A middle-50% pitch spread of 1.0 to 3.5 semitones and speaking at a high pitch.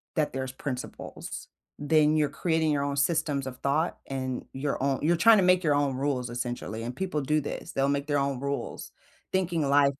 No: narrow, 2.5 semitones; medium, 140 Hz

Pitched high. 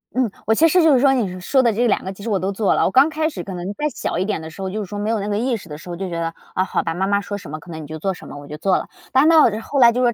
Yes: high, 200 Hz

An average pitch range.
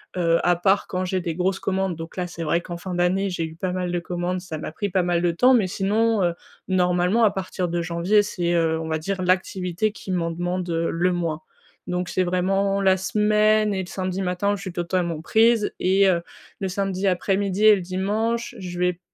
No: narrow, 2.0 semitones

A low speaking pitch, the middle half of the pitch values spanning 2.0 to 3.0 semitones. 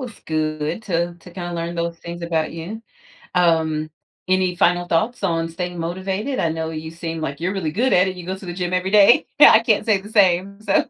No: medium, 175 Hz; average, 2.7 semitones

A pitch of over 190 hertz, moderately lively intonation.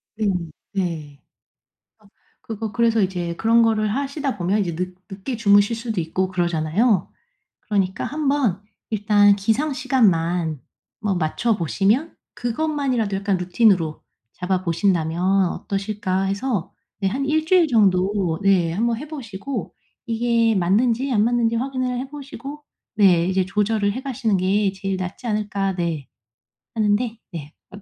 Yes: high, 205 Hz; average, 4.2 semitones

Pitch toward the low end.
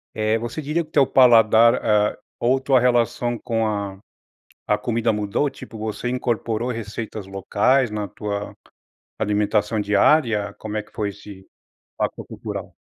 Yes: low, 110 Hz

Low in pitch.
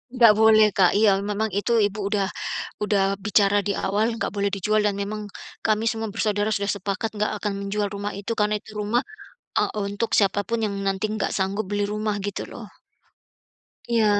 No: high, 210 Hz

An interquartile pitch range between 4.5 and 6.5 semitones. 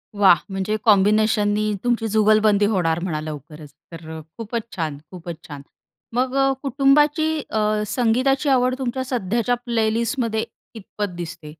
Yes: average, 4.9 semitones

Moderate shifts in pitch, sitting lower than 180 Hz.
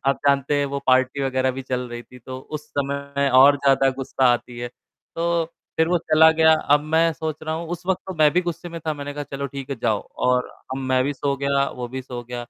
Yes: average, 3.1 semitones; medium, 140 Hz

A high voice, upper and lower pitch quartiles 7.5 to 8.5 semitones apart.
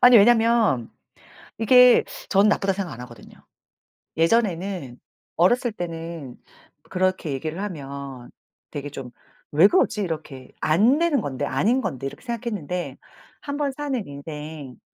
No: medium, 175 Hz; wide, 8.0 semitones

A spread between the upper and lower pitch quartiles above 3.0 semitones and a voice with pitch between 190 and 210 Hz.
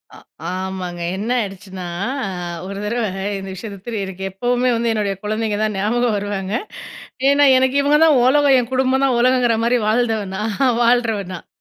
No: average, 3.9 semitones; high, 225 Hz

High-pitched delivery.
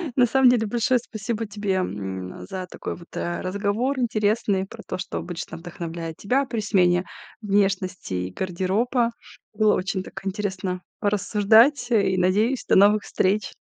Yes: high, 200 Hz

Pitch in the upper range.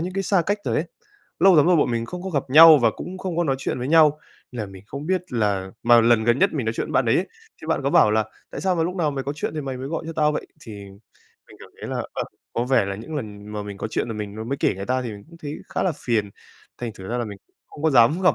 No: low, 135 Hz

